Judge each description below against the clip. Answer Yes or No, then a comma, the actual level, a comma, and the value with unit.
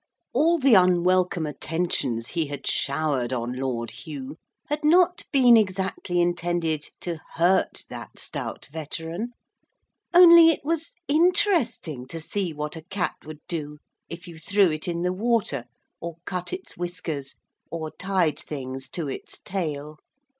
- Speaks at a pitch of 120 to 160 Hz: No, medium, 175 Hz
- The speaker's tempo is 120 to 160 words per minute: Yes, average, 140 wpm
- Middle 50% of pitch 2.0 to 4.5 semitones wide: No, average, 5.2 semitones